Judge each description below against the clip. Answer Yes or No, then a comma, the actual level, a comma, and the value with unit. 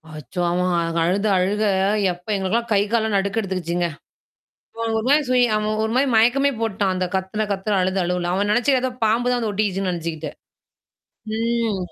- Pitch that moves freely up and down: No, average, 3.8 semitones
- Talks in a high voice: Yes, high, 200 Hz